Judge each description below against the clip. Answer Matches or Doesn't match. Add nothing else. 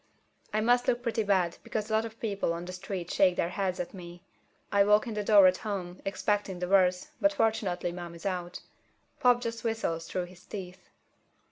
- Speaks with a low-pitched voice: Doesn't match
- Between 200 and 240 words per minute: Matches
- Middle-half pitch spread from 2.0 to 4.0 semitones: Matches